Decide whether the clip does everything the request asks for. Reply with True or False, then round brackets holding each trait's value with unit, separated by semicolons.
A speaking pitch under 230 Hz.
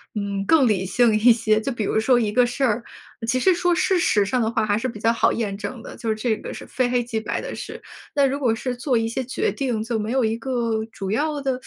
False (235 Hz)